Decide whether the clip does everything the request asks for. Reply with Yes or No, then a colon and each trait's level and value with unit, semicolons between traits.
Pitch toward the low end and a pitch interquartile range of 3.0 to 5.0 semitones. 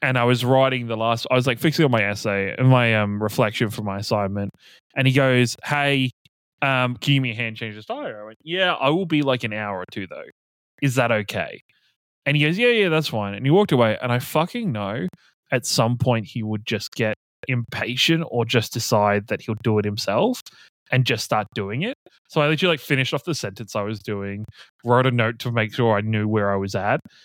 Yes: low, 120 Hz; average, 4.6 semitones